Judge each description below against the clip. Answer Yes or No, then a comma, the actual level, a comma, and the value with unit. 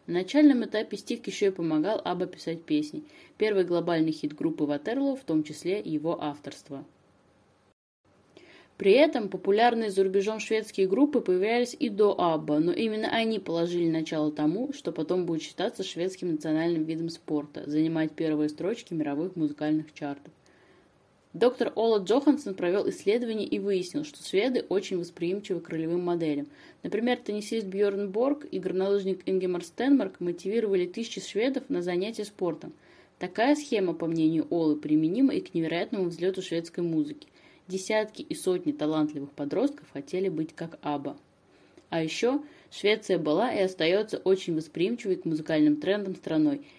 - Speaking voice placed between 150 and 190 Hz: Yes, medium, 185 Hz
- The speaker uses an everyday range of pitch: No, wide, 5.8 semitones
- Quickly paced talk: No, average, 145 wpm